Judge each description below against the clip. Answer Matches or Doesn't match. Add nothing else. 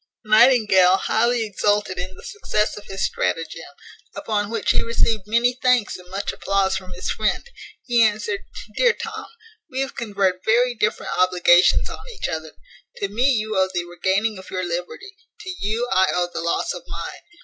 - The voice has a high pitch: Matches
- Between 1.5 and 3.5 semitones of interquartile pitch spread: Doesn't match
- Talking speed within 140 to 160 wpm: Doesn't match